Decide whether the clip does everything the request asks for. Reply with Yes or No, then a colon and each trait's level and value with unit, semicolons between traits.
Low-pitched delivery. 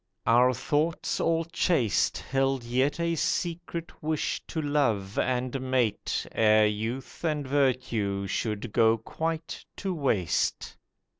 Yes: low, 130 Hz